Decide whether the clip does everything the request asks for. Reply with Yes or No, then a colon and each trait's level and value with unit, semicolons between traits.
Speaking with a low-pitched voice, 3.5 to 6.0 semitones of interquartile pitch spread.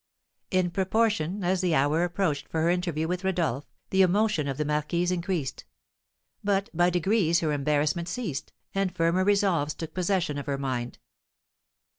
No: medium, 175 Hz; average, 3.9 semitones